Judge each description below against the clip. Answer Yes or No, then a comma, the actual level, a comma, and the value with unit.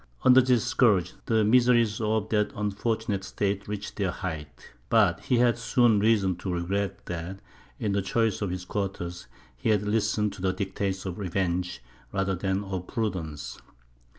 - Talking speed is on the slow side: No, average, 160 wpm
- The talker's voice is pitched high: No, low, 100 Hz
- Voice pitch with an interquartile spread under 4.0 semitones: Yes, average, 3.0 semitones